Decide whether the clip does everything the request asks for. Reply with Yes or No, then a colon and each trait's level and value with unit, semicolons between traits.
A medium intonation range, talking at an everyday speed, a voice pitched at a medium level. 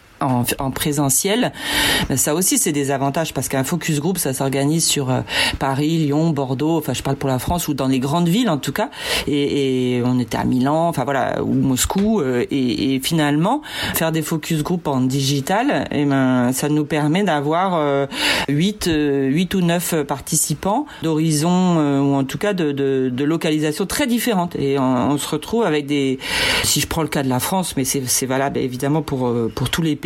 Yes: average, 3.3 semitones; average, 195 wpm; medium, 145 Hz